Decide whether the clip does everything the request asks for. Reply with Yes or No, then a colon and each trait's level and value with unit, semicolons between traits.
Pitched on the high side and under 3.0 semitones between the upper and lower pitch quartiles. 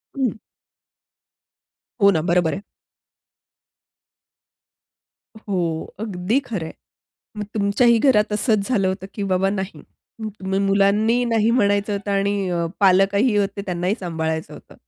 Yes: high, 200 Hz; narrow, 2.4 semitones